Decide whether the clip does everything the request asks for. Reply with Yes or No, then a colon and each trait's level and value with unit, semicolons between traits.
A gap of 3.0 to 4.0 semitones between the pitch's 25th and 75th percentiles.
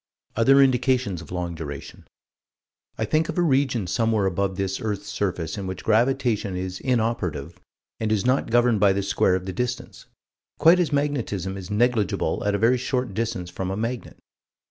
No: average, 4.8 semitones